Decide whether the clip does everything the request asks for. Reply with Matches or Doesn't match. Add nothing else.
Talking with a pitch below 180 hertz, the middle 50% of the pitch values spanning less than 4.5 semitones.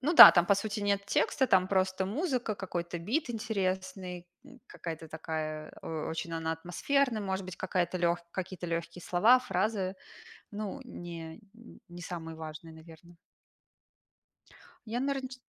Doesn't match